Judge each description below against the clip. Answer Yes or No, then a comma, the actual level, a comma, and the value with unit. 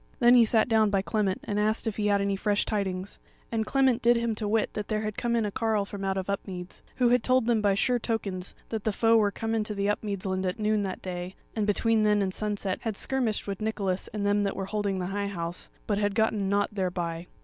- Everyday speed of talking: No, fast, 250 wpm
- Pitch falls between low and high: No, high, 210 Hz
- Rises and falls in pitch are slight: Yes, narrow, 2.2 semitones